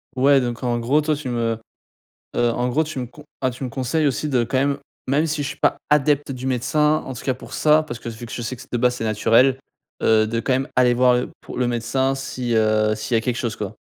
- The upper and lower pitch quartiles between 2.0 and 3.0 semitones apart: Yes, average, 2.7 semitones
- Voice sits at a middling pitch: No, low, 125 Hz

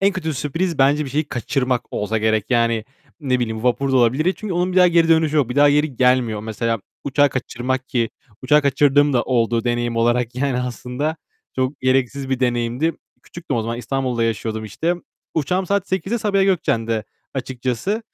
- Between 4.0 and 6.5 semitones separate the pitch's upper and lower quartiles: Yes, average, 4.3 semitones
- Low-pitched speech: Yes, low, 130 Hz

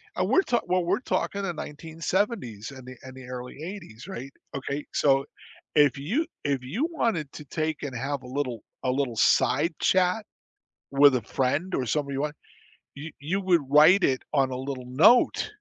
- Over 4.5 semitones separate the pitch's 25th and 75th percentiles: Yes, wide, 5.4 semitones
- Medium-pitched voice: Yes, medium, 145 Hz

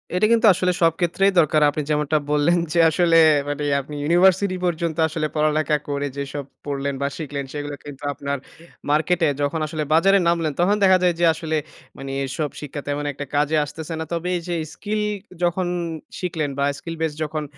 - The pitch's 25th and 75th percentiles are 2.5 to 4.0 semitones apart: Yes, average, 3.0 semitones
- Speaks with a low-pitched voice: No, medium, 155 Hz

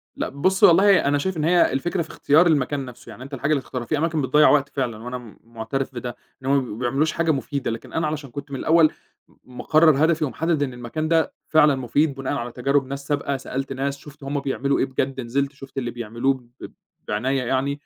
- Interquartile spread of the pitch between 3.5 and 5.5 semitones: No, average, 2.8 semitones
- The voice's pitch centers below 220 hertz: Yes, medium, 140 Hz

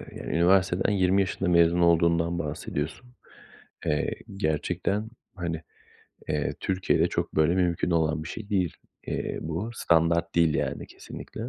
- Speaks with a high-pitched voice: No, very low, 85 Hz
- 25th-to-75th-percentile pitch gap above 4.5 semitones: No, narrow, 2.4 semitones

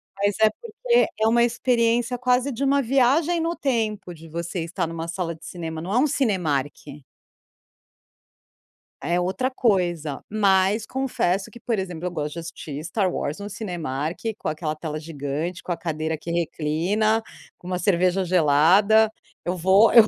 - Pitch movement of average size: No, wide, 5.7 semitones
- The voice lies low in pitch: No, medium, 185 Hz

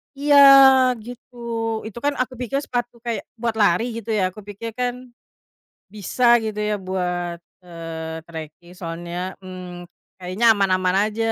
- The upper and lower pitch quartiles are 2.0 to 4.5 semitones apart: No, average, 5.0 semitones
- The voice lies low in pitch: No, high, 190 Hz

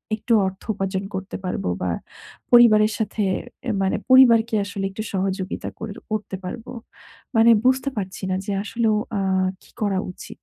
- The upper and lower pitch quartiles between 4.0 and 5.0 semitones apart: No, average, 3.0 semitones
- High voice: Yes, high, 210 Hz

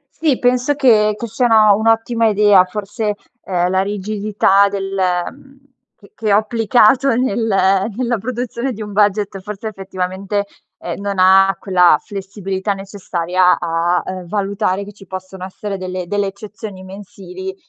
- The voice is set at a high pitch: Yes, high, 200 Hz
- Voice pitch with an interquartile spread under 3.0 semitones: Yes, narrow, 2.5 semitones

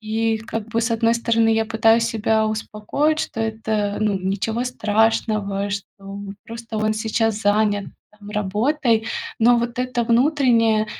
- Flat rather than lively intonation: Yes, narrow, 1.5 semitones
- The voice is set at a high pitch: Yes, high, 225 Hz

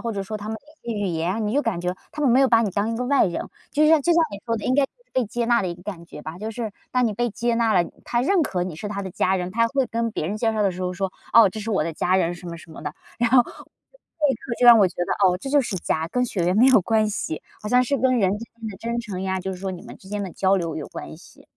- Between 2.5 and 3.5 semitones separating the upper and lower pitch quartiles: No, average, 4.4 semitones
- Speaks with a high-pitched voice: Yes, high, 215 Hz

